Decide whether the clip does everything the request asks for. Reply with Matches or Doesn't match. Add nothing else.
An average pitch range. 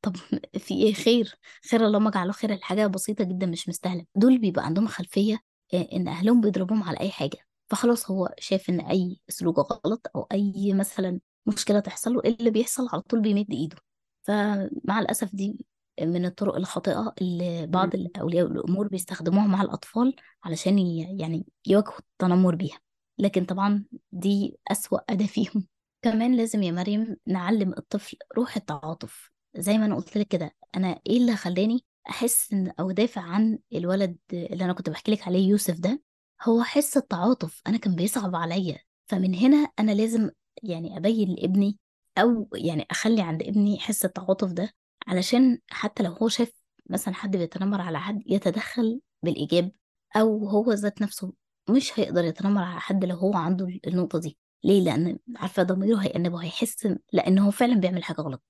Matches